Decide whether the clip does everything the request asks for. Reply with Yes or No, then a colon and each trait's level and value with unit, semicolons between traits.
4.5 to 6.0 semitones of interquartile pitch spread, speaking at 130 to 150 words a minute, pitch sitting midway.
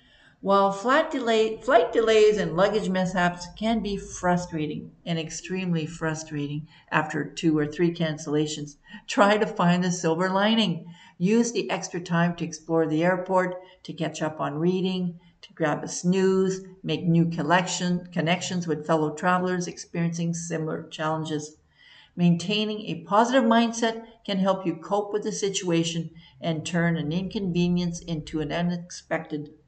No: average, 3.1 semitones; average, 140 wpm; medium, 175 Hz